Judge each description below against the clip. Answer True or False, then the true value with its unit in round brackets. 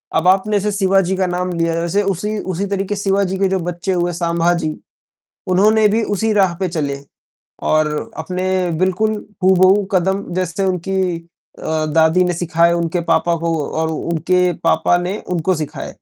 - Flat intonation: True (2.3 semitones)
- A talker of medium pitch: True (180 Hz)